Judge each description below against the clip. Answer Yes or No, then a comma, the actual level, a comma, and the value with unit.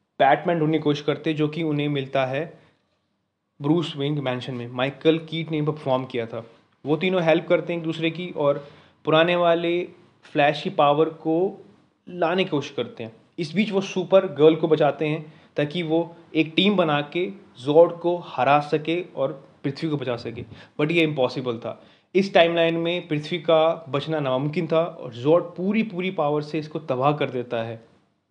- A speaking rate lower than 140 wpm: No, average, 180 wpm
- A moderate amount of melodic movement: Yes, average, 3.1 semitones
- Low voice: No, medium, 155 Hz